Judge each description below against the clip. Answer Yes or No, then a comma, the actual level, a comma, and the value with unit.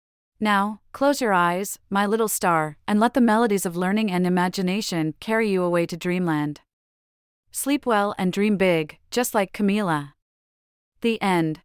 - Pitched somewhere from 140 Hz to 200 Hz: Yes, high, 190 Hz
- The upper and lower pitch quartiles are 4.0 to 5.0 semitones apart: Yes, average, 4.7 semitones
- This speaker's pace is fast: No, average, 155 wpm